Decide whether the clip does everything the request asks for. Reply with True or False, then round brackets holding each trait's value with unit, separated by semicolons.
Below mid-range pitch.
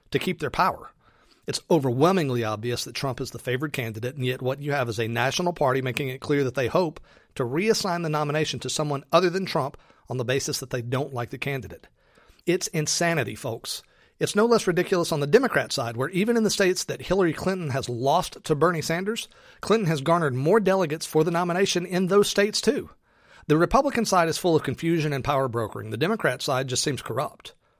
False (150 Hz)